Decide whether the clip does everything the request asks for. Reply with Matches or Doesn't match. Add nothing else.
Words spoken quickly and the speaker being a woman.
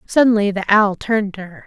Matches